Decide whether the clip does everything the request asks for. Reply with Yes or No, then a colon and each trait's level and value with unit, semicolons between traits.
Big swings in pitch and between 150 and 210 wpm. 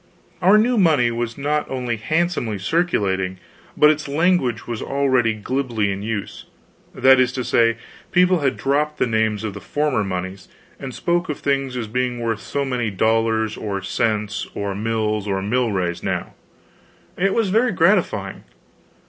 Yes: wide, 5.8 semitones; average, 155 wpm